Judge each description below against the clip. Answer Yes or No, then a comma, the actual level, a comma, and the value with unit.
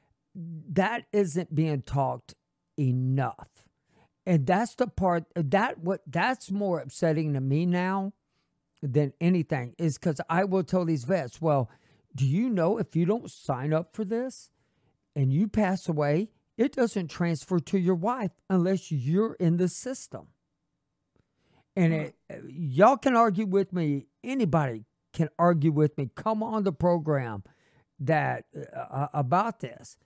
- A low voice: No, medium, 170 Hz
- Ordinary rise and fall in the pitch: Yes, average, 4.7 semitones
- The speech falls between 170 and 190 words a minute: No, average, 145 wpm